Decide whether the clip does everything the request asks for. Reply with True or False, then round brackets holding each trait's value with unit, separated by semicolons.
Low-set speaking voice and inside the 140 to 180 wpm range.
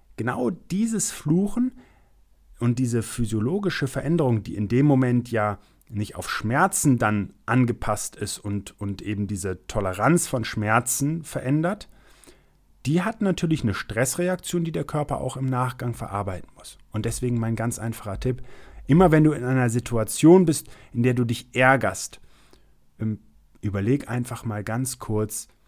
True (125 Hz; 145 wpm)